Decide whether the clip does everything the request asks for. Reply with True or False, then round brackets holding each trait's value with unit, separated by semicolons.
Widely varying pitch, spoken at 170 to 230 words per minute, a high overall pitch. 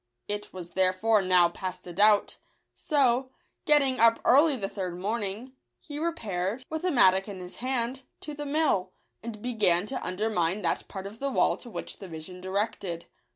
True (5.7 semitones; 180 wpm; 210 Hz)